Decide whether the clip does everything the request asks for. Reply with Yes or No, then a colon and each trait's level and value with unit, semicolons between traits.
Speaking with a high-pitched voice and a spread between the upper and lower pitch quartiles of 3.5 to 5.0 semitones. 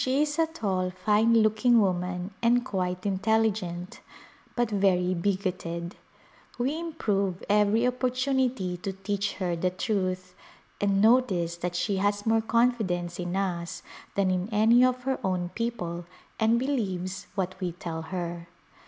Yes: high, 195 Hz; average, 4.4 semitones